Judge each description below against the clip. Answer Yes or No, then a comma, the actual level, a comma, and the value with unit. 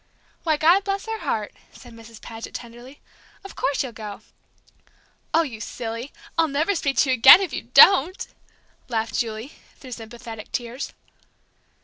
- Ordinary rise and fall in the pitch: No, wide, 5.7 semitones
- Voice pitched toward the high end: Yes, very high, 250 Hz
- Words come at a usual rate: Yes, average, 150 wpm